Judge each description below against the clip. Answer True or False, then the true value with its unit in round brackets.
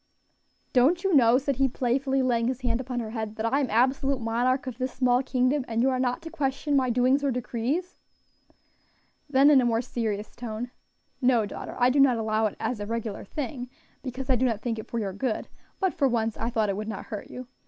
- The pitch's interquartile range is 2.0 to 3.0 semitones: True (2.7 semitones)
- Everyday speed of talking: False (225 wpm)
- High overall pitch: True (250 Hz)